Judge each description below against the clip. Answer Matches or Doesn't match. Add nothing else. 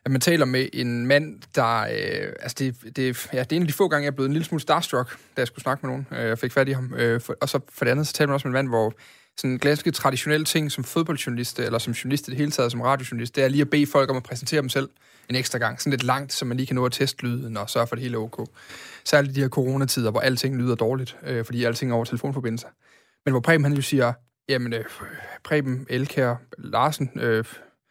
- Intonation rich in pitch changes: Doesn't match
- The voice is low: Matches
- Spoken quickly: Matches